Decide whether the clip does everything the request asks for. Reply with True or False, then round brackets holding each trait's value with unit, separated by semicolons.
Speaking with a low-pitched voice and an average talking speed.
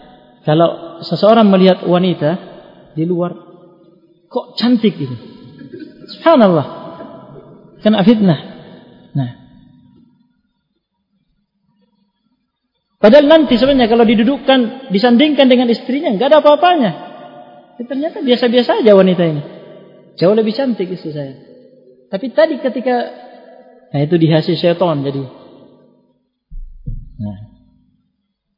False (200 Hz; 95 wpm)